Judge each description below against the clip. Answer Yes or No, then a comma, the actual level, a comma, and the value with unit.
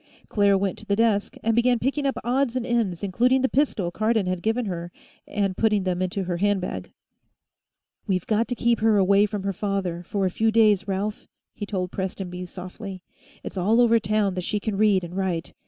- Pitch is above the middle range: Yes, high, 200 Hz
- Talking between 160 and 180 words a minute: No, fast, 205 wpm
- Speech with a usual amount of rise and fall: Yes, average, 3.3 semitones